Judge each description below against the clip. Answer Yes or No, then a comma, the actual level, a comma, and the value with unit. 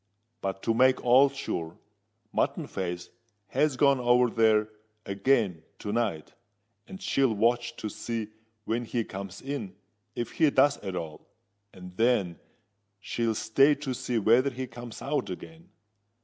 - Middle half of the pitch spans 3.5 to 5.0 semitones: Yes, average, 4.7 semitones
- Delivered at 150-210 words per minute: No, average, 140 wpm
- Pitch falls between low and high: No, low, 115 Hz